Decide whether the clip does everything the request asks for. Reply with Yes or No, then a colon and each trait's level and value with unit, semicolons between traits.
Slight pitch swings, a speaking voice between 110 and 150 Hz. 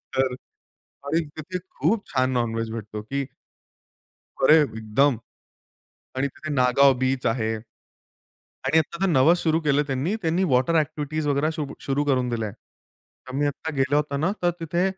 No: average, 3.3 semitones; medium, 140 Hz